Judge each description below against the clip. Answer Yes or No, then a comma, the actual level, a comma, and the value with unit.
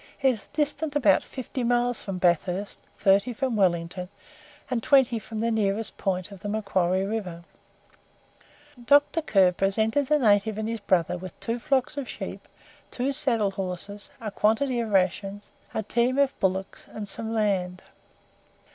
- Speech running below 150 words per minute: No, average, 155 wpm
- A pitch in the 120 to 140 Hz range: No, high, 215 Hz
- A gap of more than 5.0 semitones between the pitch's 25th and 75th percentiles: No, average, 4.2 semitones